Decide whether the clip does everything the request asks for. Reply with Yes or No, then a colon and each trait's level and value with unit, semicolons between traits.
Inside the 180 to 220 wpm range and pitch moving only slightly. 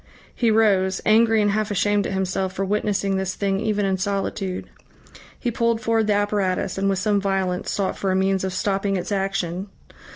Yes: average, 190 wpm; narrow, 1.6 semitones